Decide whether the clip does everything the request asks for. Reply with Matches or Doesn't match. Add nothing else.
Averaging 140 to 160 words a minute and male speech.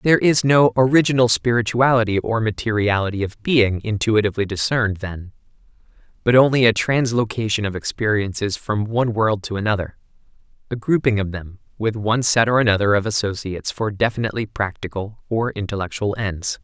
Matches